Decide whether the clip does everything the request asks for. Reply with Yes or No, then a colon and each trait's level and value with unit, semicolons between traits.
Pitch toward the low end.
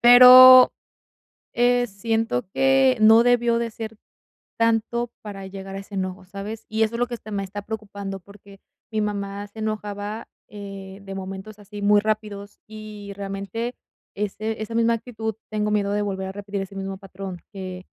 No: high, 210 Hz